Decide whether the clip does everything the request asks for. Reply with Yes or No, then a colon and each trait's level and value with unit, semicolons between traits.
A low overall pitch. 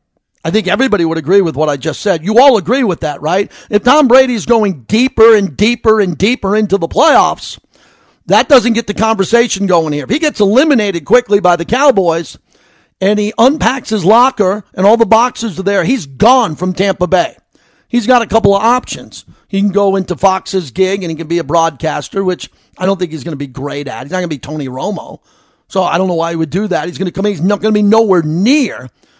No: high, 200 Hz